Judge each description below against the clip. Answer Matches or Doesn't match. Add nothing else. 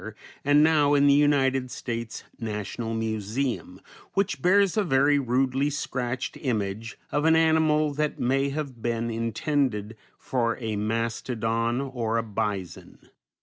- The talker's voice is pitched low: Matches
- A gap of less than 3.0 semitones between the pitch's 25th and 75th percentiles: Doesn't match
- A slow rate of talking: Matches